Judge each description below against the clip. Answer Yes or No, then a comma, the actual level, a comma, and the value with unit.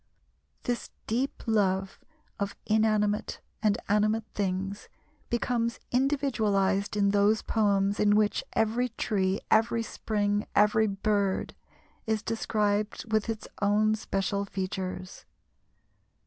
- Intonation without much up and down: Yes, narrow, 1.7 semitones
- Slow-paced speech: Yes, slow, 105 wpm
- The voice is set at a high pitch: Yes, high, 210 Hz